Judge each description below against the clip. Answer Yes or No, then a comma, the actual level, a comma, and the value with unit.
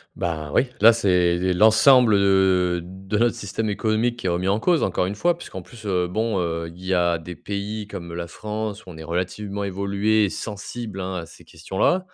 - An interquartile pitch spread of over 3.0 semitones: Yes, average, 3.4 semitones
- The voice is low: Yes, low, 100 Hz